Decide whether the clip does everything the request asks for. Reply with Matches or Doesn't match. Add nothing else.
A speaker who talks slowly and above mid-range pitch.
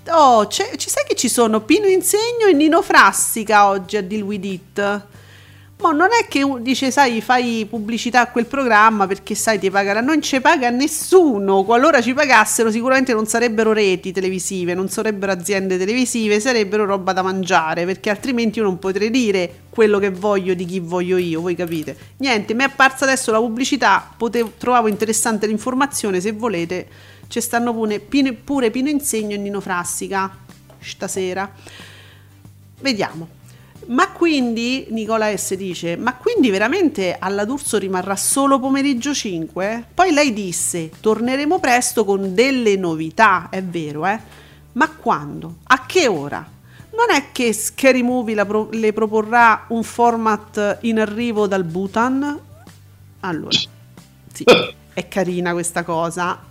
Doesn't match